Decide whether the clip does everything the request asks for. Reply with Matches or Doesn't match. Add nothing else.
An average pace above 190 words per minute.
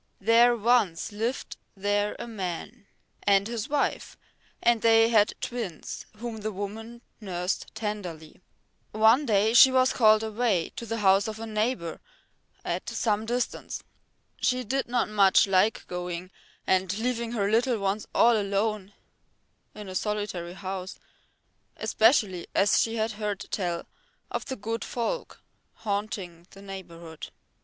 Doesn't match